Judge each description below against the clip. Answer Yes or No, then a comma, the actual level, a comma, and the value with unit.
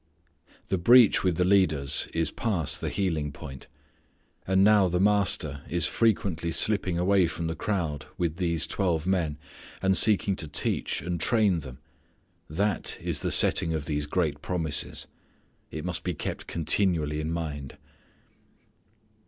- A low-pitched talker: Yes, very low, 85 Hz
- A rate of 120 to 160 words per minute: Yes, average, 145 wpm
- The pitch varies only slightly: No, average, 3.8 semitones